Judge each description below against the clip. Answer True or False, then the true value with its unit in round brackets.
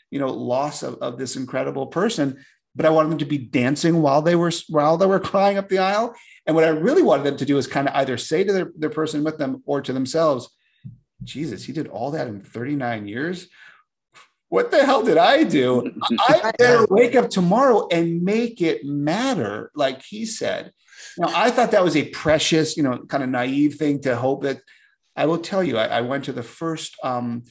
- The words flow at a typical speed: False (220 wpm)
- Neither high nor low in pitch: True (155 Hz)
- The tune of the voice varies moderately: False (5.8 semitones)